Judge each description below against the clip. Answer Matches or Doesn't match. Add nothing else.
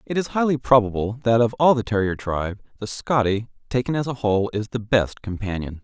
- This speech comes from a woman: Doesn't match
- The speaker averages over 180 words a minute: Matches